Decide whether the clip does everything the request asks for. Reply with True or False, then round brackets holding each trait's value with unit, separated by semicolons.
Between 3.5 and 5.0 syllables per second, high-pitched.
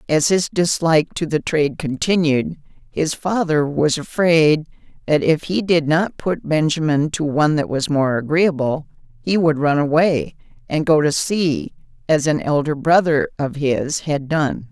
False (4.3 syllables/s; 155 Hz)